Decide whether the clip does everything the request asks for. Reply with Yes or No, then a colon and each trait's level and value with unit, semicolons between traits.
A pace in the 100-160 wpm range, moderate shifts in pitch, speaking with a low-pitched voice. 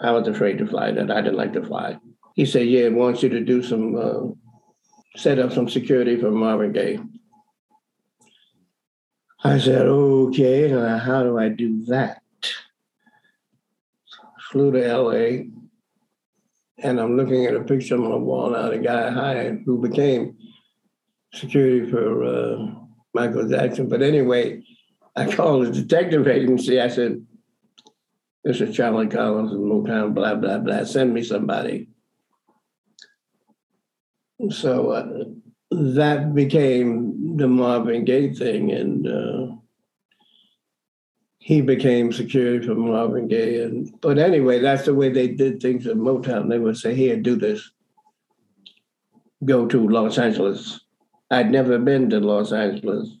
Yes: average, 140 wpm; average, 4.7 semitones; low, 130 Hz